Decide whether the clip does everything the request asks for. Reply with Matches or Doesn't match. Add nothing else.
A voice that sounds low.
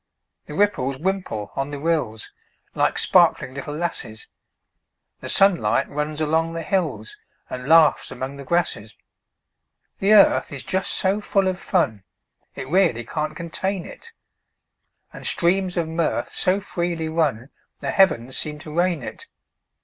Doesn't match